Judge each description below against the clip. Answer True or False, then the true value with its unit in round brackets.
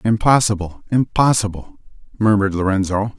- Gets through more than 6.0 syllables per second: False (5.4 syllables/s)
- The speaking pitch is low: True (105 Hz)